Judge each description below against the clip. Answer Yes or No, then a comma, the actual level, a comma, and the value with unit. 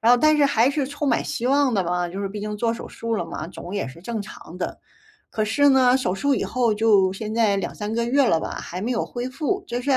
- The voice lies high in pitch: Yes, high, 230 Hz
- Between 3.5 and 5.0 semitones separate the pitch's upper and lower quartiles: Yes, average, 4.7 semitones